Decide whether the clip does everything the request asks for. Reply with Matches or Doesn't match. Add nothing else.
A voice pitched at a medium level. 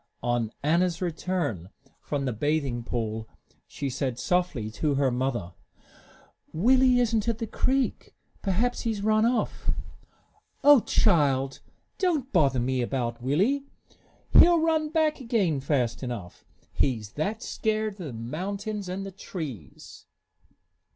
Matches